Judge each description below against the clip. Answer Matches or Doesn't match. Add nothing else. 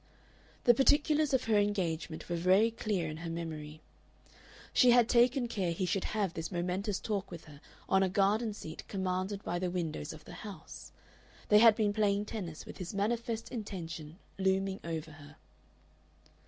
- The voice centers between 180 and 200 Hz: Matches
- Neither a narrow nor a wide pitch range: Matches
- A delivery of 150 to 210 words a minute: Matches